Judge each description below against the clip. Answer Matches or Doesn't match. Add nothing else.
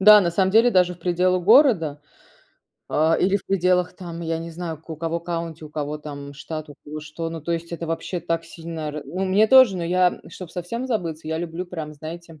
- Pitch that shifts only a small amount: Matches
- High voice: Doesn't match